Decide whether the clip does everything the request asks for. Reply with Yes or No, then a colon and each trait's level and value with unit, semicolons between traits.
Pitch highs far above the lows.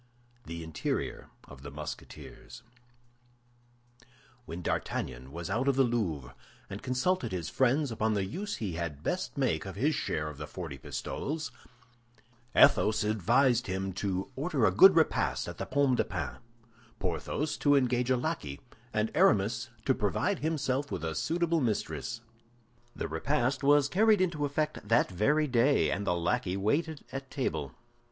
Yes: wide, 8.2 semitones